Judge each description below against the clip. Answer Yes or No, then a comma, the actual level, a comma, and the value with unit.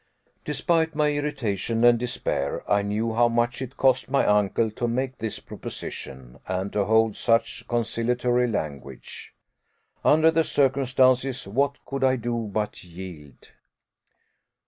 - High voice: No, low, 120 Hz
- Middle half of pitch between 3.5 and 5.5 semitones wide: Yes, average, 4.2 semitones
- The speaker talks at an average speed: No, slow, 130 wpm